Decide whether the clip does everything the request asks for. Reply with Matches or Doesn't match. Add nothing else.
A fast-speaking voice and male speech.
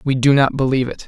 Matches